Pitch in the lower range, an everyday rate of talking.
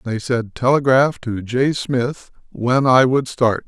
Yes: low, 125 Hz; average, 165 wpm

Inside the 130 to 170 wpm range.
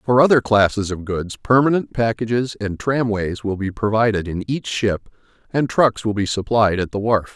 No: average, 190 wpm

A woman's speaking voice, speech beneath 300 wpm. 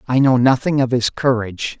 No: male; average, 200 wpm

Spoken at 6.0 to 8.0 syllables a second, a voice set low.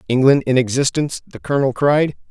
Yes: 6.1 syllables/s; low, 130 Hz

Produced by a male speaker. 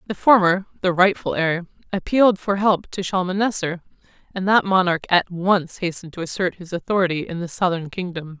No: female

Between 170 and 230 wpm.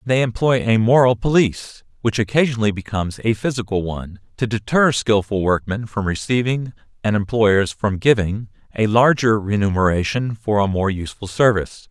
No: average, 150 wpm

